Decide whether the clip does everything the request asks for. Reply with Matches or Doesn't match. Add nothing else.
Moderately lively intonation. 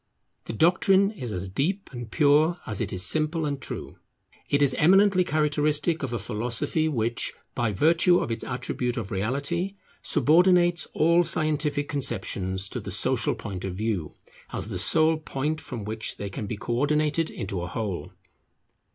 Doesn't match